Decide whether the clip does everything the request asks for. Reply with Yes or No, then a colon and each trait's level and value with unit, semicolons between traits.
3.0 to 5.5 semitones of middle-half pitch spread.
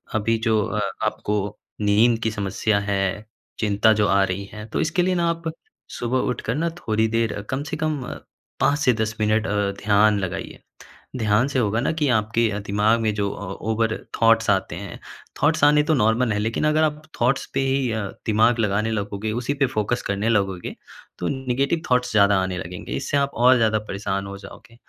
Yes: average, 3.6 semitones